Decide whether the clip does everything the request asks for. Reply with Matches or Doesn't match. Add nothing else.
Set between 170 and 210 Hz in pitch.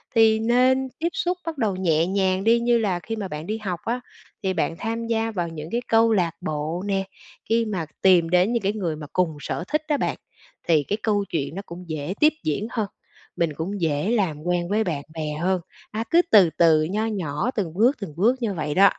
Matches